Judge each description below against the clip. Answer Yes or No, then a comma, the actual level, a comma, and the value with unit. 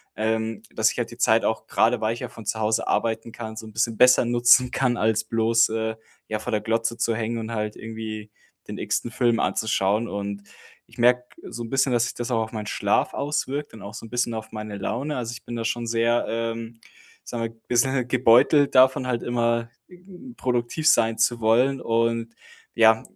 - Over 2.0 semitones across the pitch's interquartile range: No, narrow, 1.4 semitones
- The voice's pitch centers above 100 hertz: Yes, low, 115 Hz